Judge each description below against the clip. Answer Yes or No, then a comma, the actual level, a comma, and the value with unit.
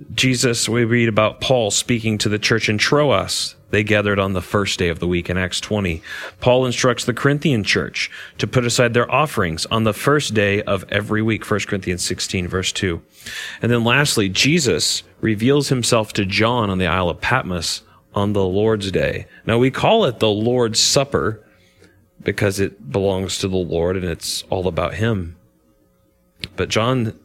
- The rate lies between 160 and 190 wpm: Yes, average, 180 wpm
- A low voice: Yes, low, 105 Hz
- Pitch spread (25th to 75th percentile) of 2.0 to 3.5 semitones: No, average, 4.3 semitones